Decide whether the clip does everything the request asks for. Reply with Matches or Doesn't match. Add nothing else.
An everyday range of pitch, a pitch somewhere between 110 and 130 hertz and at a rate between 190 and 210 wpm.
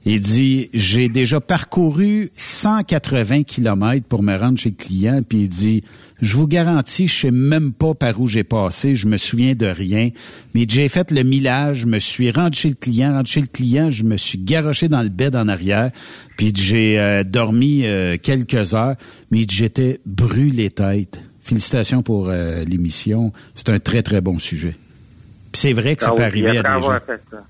Matches